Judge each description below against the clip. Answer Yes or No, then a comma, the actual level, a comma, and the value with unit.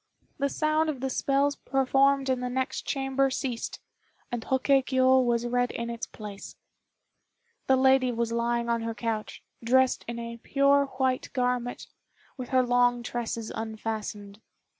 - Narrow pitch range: Yes, narrow, 2.3 semitones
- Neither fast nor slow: Yes, average, 150 wpm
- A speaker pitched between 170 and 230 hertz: No, very high, 250 Hz